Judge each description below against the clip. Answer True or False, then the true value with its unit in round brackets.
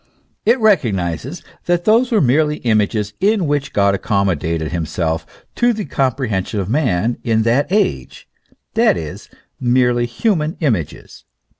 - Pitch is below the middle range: True (120 Hz)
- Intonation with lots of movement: True (8.2 semitones)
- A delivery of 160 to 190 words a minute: False (135 wpm)